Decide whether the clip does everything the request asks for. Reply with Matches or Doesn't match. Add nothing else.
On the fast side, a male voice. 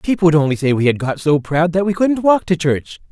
Matches